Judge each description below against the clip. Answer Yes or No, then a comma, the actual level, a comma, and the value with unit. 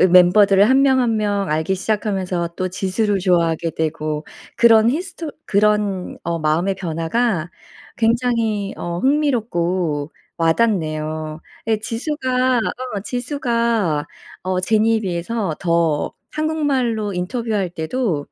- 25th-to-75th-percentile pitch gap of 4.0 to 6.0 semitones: Yes, wide, 5.4 semitones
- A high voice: Yes, high, 200 Hz